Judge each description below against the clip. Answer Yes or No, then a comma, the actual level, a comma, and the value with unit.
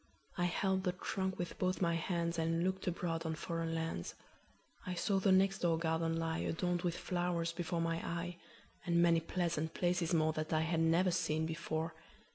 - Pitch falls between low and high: Yes, medium, 170 Hz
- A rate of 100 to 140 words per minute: No, average, 160 wpm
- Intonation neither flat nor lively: No, narrow, 1.6 semitones